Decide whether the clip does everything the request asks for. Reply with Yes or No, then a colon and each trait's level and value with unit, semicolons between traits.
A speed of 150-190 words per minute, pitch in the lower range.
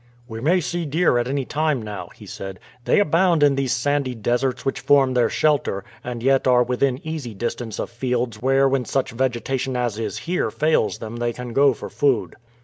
No: average, 200 wpm; low, 130 Hz